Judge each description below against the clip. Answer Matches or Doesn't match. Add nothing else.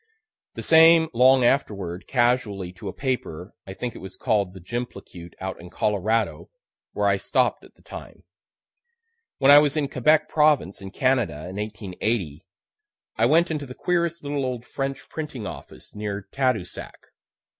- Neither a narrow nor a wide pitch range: Doesn't match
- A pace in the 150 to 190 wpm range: Matches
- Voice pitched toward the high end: Doesn't match